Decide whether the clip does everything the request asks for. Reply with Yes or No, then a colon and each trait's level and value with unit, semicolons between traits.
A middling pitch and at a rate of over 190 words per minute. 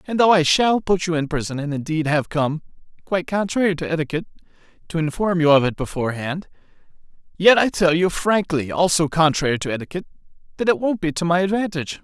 No: medium, 165 Hz; average, 180 wpm